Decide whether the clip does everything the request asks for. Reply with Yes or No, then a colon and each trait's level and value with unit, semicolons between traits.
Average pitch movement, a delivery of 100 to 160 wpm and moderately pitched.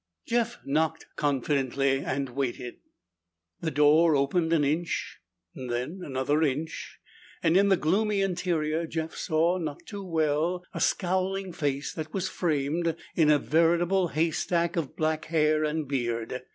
Yes: average, 3.3 semitones; average, 140 wpm; medium, 160 Hz